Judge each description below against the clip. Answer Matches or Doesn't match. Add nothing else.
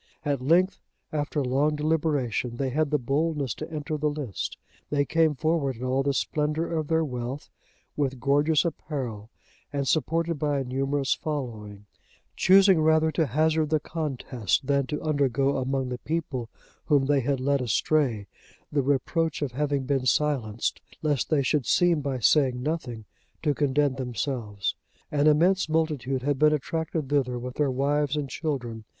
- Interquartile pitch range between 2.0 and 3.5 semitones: Matches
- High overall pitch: Doesn't match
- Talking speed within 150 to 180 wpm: Matches